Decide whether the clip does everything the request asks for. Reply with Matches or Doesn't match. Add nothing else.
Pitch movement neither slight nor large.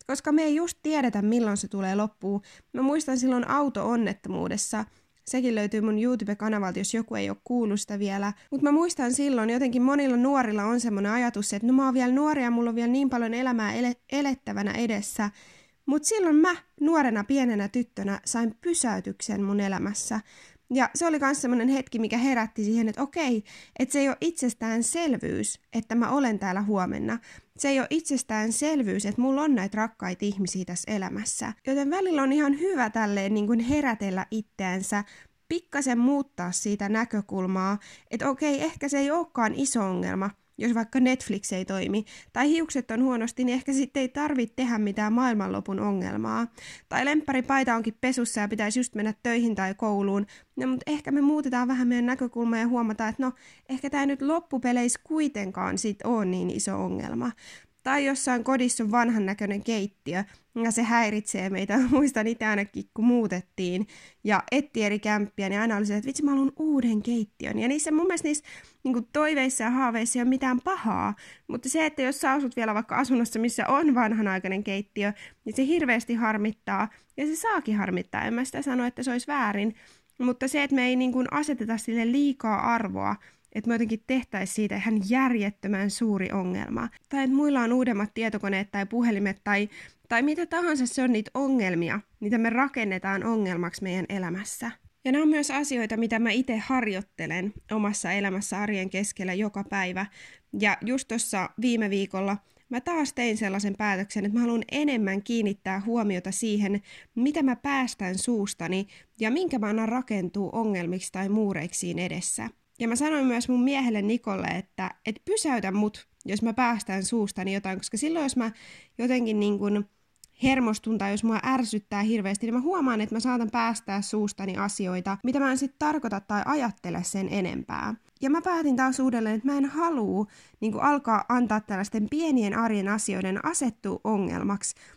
Matches